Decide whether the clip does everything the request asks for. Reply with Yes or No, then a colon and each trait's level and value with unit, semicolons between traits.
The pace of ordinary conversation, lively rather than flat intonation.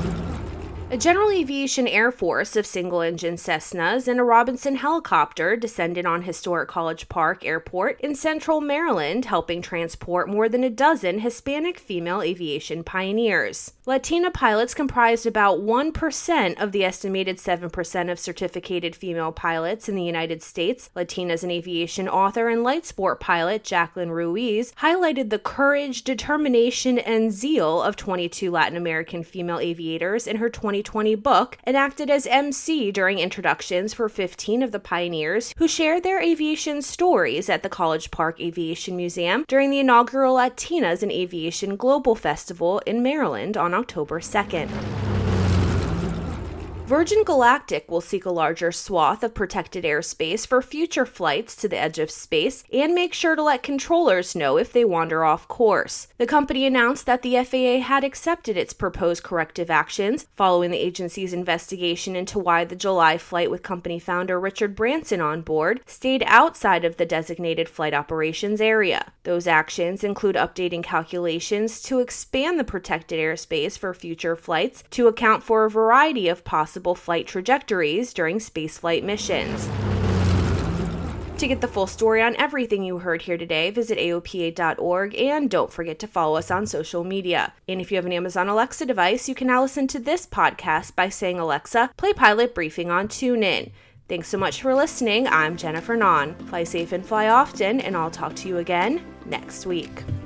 Yes: average, 160 wpm; wide, 6.7 semitones